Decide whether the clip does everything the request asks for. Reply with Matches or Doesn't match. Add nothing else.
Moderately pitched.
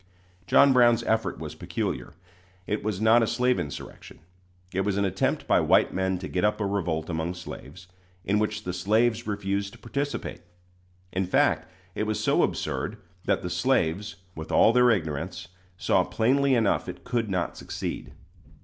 Doesn't match